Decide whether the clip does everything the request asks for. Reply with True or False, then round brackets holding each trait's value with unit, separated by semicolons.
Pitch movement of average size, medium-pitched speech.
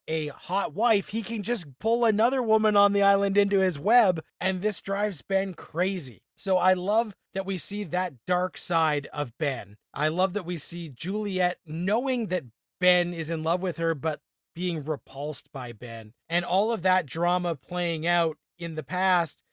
True (3.8 semitones; 180 Hz)